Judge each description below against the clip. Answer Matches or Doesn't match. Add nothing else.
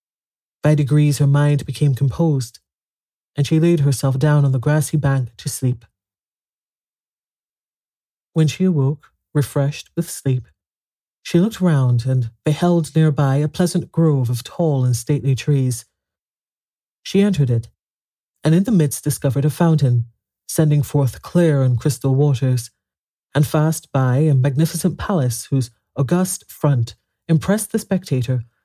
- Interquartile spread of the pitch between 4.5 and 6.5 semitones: Doesn't match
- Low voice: Doesn't match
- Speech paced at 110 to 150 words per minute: Matches